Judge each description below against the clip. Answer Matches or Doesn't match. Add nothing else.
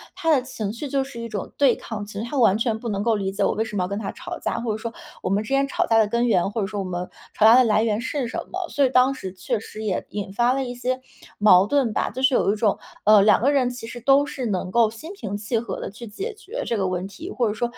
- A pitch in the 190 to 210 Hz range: Doesn't match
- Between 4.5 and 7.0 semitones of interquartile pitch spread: Doesn't match